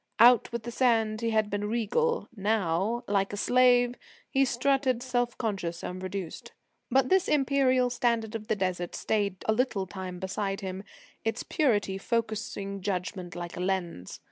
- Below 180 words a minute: Yes, average, 160 wpm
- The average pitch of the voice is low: No, high, 215 Hz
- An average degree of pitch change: Yes, average, 4.2 semitones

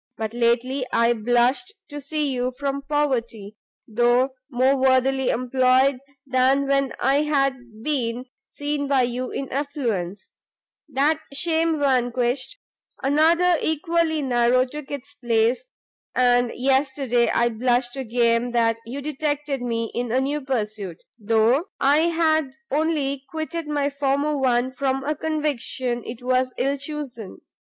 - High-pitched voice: Yes, very high, 265 Hz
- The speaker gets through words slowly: Yes, slow, 130 wpm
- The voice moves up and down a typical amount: Yes, average, 3.0 semitones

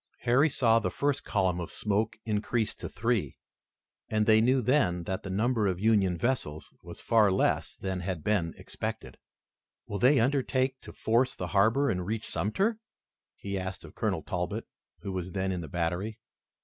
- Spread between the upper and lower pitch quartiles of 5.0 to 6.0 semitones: No, average, 4.4 semitones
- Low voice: Yes, low, 105 Hz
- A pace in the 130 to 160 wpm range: No, average, 175 wpm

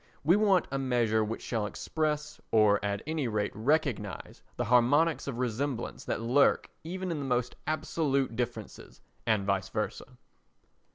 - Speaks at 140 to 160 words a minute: Yes, average, 150 wpm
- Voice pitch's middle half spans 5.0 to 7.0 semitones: Yes, wide, 5.4 semitones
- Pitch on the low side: Yes, low, 125 Hz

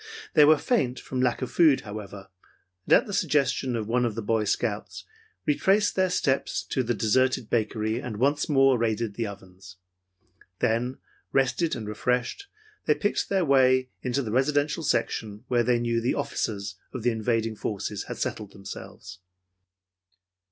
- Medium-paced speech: Yes, average, 160 wpm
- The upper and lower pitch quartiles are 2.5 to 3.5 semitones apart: No, average, 4.0 semitones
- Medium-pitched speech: No, low, 120 Hz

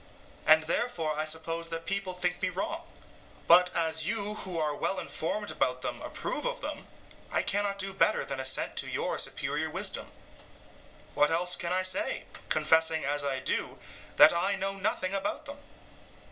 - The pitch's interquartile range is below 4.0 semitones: Yes, average, 3.6 semitones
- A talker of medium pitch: Yes, medium, 180 Hz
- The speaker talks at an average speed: Yes, average, 170 wpm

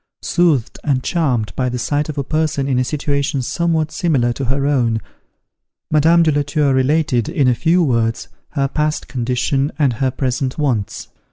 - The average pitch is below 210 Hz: Yes, medium, 140 Hz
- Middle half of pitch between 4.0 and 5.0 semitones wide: No, average, 3.4 semitones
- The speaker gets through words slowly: No, average, 175 wpm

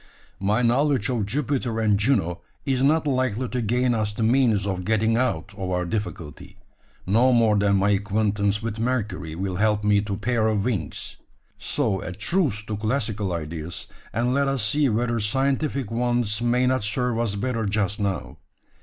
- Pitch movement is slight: No, average, 3.7 semitones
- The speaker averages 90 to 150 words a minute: No, average, 175 wpm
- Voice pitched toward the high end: No, low, 110 Hz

